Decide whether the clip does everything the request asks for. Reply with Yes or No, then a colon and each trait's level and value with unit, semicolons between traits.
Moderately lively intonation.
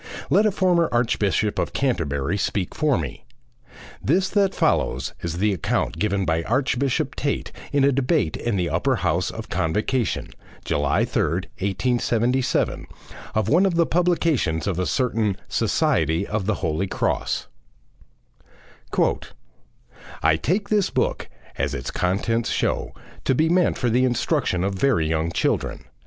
No: wide, 7.8 semitones